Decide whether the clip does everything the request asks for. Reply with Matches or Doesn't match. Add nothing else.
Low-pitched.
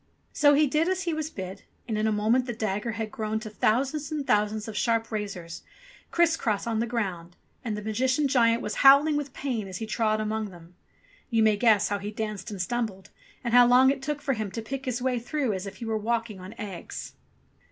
Doesn't match